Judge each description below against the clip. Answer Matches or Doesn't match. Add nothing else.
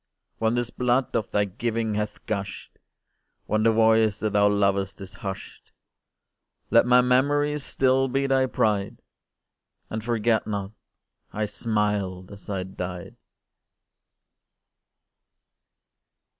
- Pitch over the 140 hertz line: Doesn't match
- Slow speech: Matches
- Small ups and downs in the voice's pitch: Doesn't match